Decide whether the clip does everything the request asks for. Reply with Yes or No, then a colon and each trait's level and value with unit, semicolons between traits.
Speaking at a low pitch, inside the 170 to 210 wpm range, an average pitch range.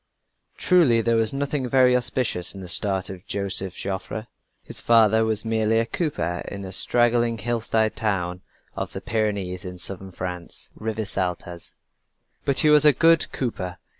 No: low, 110 Hz; average, 155 wpm; average, 4.1 semitones